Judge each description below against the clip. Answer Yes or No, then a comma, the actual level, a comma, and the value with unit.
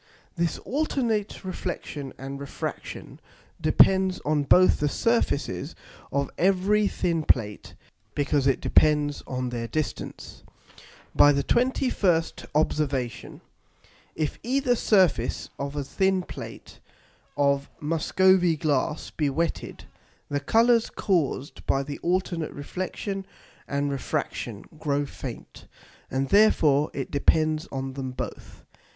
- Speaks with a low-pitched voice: No, medium, 155 Hz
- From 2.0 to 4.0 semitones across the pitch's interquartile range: No, average, 5.1 semitones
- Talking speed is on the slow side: Yes, slow, 110 wpm